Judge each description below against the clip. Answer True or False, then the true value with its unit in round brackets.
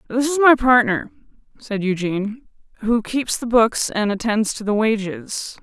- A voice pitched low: False (225 Hz)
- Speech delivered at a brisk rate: False (160 wpm)